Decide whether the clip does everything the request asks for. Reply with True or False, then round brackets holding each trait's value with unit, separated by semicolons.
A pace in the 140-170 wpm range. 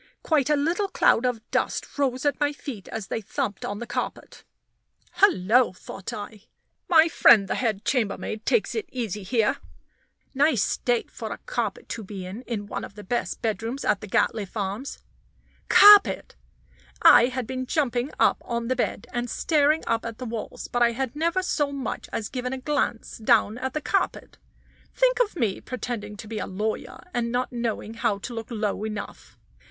False (185 wpm)